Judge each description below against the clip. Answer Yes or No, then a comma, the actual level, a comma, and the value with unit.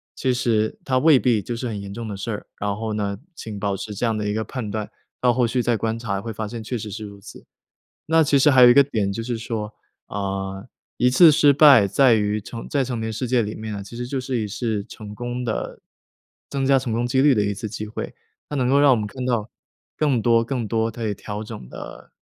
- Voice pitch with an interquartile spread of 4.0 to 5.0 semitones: No, average, 3.2 semitones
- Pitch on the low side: Yes, low, 115 Hz